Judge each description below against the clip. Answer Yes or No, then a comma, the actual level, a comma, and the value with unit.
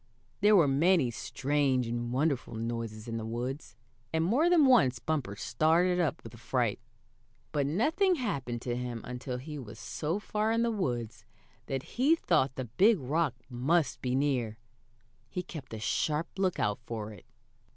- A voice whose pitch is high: No, low, 135 Hz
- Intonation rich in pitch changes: Yes, wide, 6.8 semitones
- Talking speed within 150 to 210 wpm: Yes, average, 160 wpm